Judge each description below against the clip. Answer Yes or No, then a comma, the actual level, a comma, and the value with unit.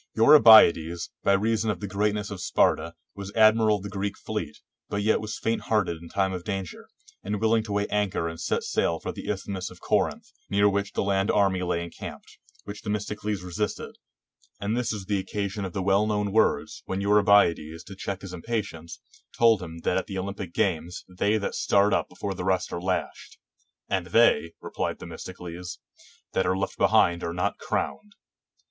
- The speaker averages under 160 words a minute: No, average, 185 wpm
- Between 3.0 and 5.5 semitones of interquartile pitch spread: No, narrow, 2.4 semitones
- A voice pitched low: Yes, low, 100 Hz